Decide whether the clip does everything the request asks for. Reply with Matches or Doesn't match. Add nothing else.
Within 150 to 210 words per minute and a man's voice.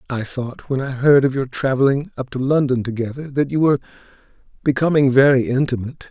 Matches